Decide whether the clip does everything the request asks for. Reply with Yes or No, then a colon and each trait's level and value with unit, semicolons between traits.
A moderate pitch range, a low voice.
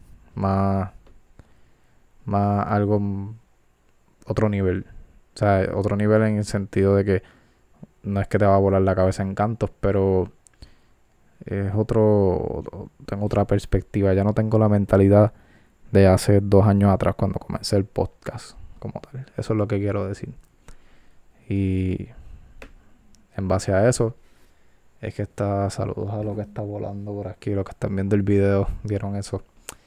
No: narrow, 1.4 semitones; low, 100 Hz